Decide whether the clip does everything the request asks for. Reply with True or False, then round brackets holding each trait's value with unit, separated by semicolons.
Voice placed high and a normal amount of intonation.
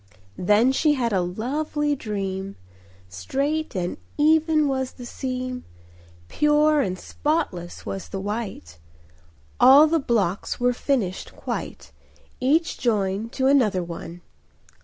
False (245 Hz; 7.2 semitones)